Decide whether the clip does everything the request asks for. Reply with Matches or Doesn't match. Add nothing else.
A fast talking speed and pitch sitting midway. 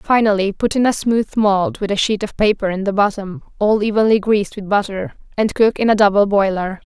Doesn't match